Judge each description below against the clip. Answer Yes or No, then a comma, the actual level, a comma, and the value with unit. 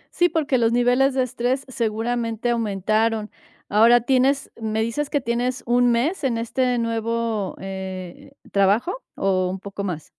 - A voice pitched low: No, high, 230 Hz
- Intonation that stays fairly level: No, average, 3.0 semitones